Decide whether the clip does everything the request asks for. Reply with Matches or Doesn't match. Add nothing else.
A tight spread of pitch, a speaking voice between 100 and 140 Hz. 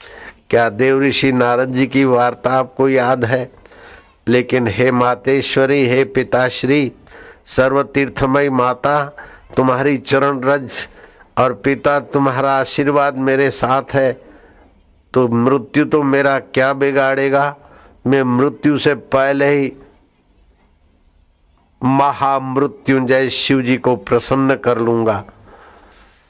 Matches